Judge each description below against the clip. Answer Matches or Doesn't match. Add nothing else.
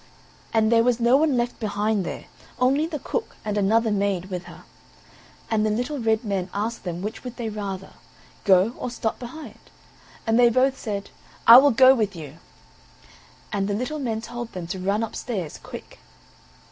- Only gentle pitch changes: Doesn't match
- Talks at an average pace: Matches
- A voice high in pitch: Matches